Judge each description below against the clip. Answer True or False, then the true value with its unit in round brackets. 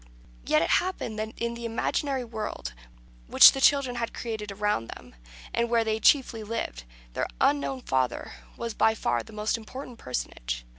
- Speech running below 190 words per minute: True (165 wpm)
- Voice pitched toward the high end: True (220 Hz)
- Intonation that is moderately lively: False (8.3 semitones)